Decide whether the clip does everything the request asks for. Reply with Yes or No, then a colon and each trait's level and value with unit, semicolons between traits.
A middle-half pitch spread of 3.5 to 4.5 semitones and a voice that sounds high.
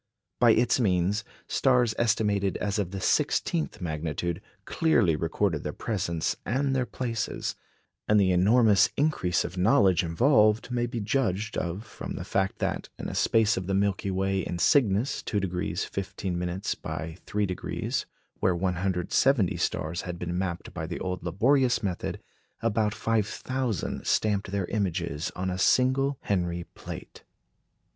No: average, 4.2 semitones; low, 100 Hz